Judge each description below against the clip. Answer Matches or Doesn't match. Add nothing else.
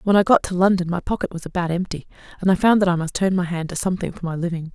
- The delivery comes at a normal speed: Doesn't match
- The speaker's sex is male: Doesn't match